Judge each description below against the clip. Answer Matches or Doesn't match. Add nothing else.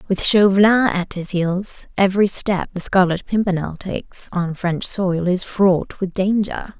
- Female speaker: Matches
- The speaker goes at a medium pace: Matches